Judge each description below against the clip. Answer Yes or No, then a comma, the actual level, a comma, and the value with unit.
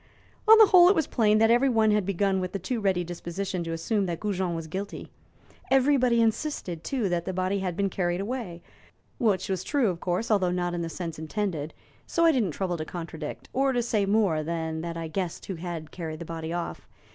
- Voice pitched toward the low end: No, high, 190 Hz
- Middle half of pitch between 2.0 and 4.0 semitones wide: No, average, 4.6 semitones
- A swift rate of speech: Yes, fast, 215 wpm